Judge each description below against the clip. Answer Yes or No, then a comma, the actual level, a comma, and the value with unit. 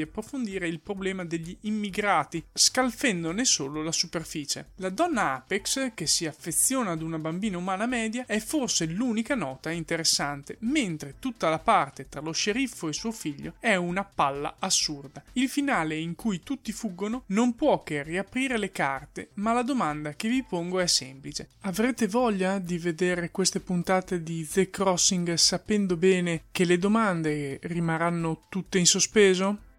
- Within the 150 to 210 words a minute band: Yes, average, 155 wpm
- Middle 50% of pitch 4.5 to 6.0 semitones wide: Yes, average, 5.2 semitones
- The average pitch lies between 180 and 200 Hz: Yes, medium, 185 Hz